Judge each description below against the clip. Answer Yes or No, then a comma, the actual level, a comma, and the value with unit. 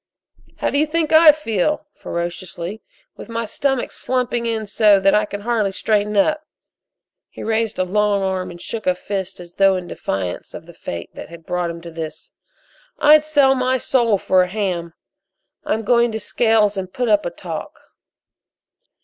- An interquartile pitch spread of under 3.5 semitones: No, average, 4.5 semitones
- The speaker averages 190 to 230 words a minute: No, average, 175 wpm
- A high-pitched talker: Yes, high, 210 Hz